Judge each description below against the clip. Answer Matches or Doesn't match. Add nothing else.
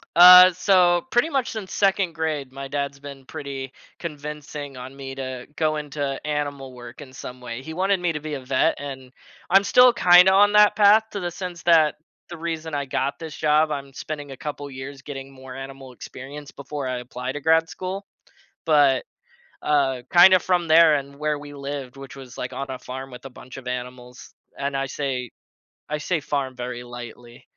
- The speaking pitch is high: Doesn't match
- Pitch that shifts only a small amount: Doesn't match